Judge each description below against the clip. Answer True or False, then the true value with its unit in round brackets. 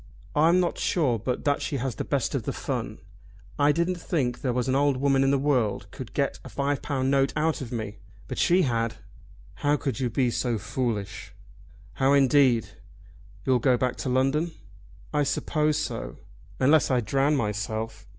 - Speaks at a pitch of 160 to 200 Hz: False (135 Hz)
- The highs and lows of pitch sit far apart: False (3.2 semitones)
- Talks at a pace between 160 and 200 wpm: True (180 wpm)